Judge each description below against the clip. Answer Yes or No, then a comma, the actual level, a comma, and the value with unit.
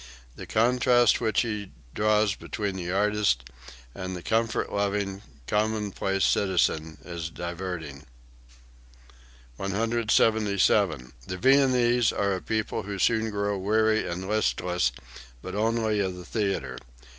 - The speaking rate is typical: No, slow, 115 wpm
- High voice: No, low, 100 Hz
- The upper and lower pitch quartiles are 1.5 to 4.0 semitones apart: Yes, average, 3.1 semitones